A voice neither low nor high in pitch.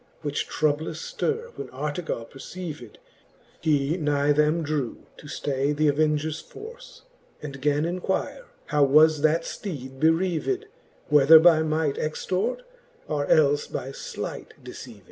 Yes: medium, 155 Hz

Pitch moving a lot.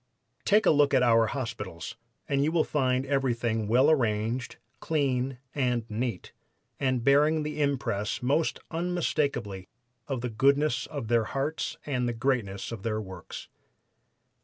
No: average, 3.8 semitones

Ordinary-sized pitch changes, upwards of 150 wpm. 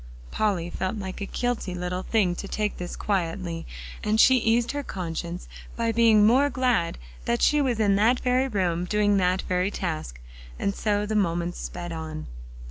Yes: average, 4.2 semitones; average, 175 wpm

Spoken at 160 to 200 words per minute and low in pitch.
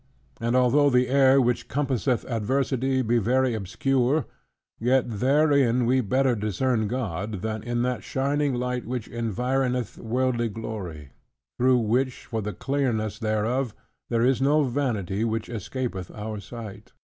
No: slow, 135 wpm; low, 120 Hz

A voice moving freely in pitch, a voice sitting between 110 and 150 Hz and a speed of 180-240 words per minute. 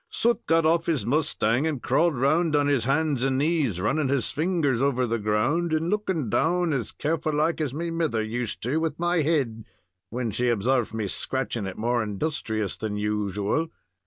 Yes: wide, 6.0 semitones; medium, 140 Hz; average, 190 wpm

